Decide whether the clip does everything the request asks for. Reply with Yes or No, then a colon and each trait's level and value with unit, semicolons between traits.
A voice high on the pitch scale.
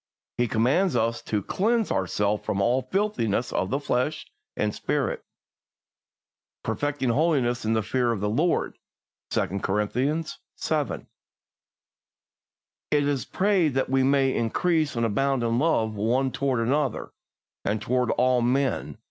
No: low, 125 Hz